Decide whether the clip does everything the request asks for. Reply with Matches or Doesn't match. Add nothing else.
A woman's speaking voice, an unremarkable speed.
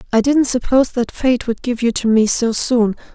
Doesn't match